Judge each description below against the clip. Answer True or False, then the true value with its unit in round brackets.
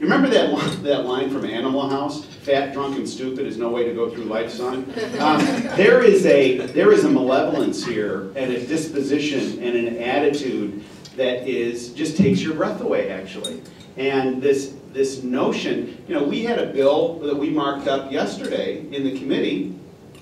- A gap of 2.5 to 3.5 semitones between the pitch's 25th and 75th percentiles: True (3.1 semitones)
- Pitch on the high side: False (135 Hz)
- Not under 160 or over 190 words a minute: True (180 wpm)